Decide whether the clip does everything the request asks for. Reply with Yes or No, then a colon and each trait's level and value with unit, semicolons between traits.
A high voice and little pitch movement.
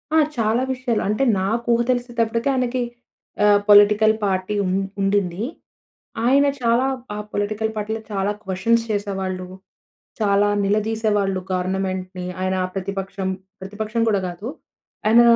No: high, 205 Hz; average, 3.0 semitones